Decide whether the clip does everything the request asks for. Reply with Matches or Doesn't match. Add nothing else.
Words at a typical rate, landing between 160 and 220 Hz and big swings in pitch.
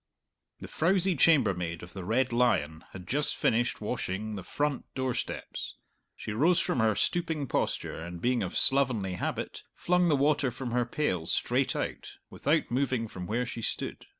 Doesn't match